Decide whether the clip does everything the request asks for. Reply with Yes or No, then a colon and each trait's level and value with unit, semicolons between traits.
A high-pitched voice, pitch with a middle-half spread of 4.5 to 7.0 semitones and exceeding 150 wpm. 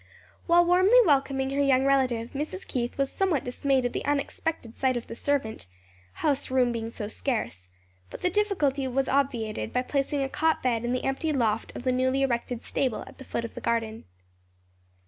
No: very high, 265 Hz; average, 3.0 semitones; average, 190 wpm